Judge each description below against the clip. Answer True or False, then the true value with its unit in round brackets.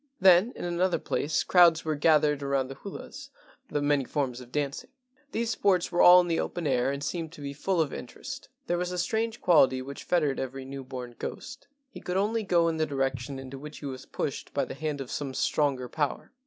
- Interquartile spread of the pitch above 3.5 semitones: True (4.6 semitones)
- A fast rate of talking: True (220 wpm)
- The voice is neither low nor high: True (150 Hz)